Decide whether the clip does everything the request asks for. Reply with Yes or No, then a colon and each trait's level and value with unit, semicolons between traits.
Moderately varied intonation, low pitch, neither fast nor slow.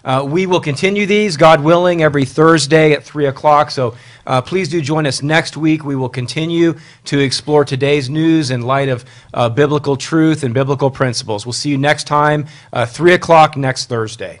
No: average, 3.3 semitones; medium, 145 Hz; average, 190 wpm